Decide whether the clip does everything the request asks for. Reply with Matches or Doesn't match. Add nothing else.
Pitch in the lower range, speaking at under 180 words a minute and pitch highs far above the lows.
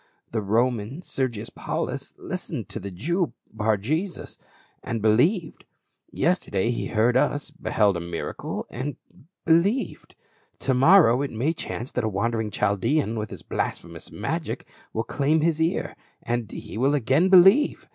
Matches